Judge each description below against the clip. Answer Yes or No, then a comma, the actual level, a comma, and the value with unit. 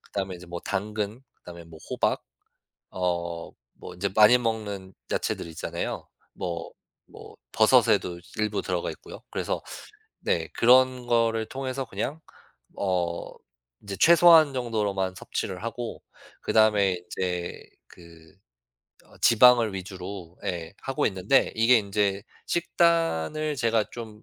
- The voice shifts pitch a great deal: No, average, 4.5 semitones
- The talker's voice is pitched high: No, low, 100 Hz